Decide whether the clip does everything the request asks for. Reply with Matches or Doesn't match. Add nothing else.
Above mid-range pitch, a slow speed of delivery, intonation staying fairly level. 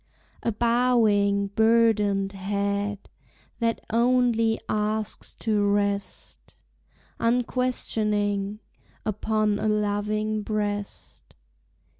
Matches